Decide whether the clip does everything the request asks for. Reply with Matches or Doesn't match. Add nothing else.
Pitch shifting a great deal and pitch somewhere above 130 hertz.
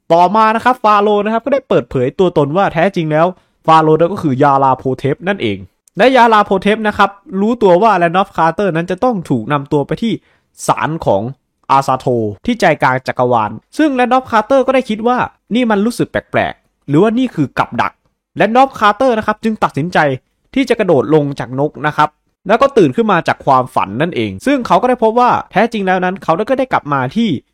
Matches